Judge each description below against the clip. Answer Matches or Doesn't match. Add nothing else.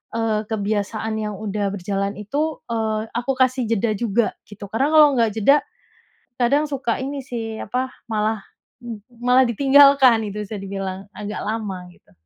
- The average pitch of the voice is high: Matches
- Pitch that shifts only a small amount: Doesn't match